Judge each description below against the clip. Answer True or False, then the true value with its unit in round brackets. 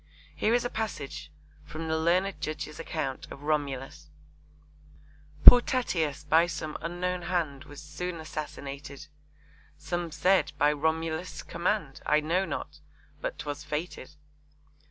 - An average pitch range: True (3.2 semitones)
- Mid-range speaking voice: True (160 Hz)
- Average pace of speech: False (125 wpm)